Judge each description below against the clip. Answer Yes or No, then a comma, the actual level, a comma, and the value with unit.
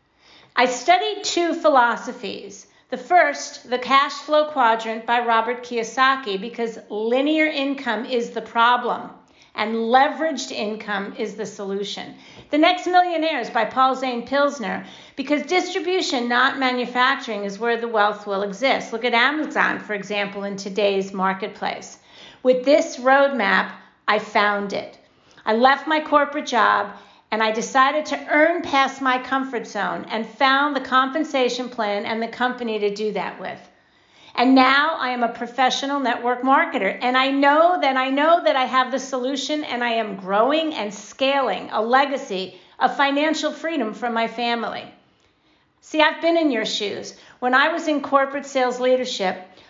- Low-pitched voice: No, very high, 255 Hz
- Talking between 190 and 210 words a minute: No, average, 155 wpm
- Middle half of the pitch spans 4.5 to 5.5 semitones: No, average, 4.0 semitones